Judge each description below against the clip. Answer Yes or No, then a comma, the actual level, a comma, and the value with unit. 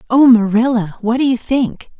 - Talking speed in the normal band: Yes, average, 180 wpm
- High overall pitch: Yes, high, 235 Hz